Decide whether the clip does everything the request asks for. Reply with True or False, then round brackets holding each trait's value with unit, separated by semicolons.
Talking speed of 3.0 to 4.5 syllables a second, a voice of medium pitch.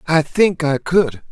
True (3.6 syllables/s; 160 Hz)